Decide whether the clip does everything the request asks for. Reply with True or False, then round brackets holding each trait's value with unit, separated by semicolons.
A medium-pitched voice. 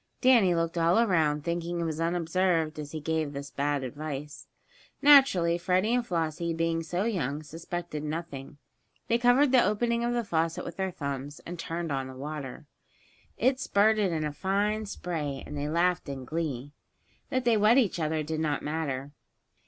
True (165 Hz)